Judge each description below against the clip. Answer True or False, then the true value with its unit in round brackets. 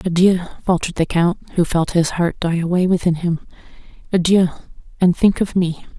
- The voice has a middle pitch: True (175 Hz)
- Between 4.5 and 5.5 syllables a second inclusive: True (5.4 syllables/s)